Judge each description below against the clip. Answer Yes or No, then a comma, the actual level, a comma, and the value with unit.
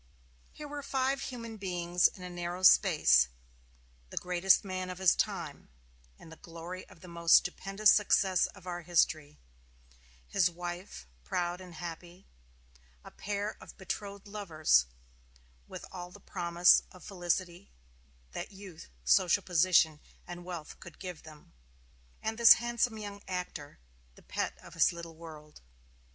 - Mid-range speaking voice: Yes, medium, 180 Hz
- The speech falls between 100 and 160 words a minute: Yes, average, 140 wpm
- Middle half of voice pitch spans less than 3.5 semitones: Yes, average, 2.7 semitones